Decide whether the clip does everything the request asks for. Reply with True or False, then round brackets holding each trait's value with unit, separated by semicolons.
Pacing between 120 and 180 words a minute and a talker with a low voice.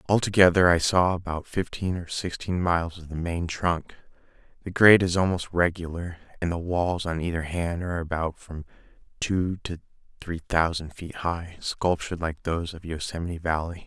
True (165 wpm; 85 Hz)